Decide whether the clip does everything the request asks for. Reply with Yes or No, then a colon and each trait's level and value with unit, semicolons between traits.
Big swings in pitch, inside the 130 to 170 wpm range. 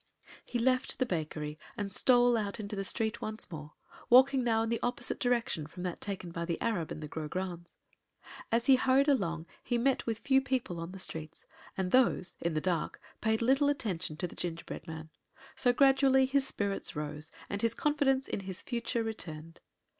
No: wide, 6.9 semitones; average, 190 wpm